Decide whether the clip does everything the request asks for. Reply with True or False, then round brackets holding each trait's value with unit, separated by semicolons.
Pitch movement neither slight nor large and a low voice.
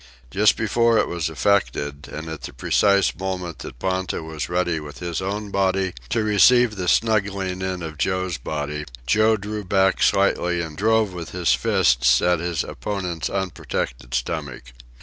True (3.8 semitones; 90 Hz)